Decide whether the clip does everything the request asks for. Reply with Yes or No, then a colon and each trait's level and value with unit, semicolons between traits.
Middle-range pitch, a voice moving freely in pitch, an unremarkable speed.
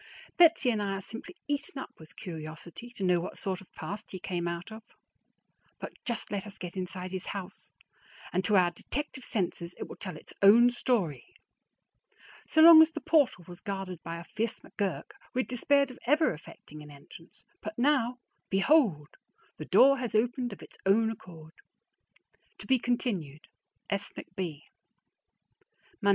No: high, 200 Hz; wide, 5.9 semitones; average, 170 wpm